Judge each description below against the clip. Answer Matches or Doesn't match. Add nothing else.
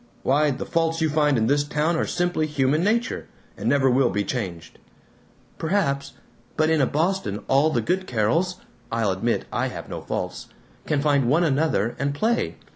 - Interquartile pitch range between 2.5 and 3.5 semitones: Doesn't match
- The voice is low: Doesn't match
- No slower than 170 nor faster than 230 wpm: Matches